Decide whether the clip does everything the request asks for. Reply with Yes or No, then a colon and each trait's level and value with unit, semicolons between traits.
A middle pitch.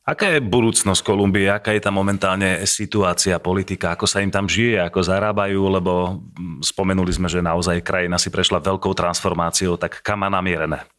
No: very low, 95 Hz